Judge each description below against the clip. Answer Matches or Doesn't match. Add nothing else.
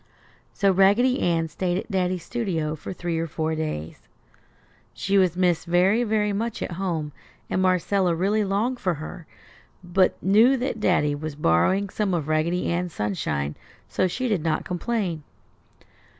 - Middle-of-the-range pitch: Matches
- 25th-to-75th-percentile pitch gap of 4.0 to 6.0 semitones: Doesn't match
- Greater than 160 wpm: Doesn't match